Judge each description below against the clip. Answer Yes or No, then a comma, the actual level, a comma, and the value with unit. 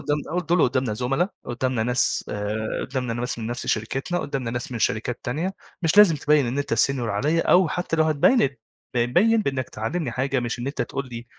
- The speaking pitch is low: Yes, low, 130 Hz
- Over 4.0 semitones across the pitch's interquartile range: Yes, average, 4.6 semitones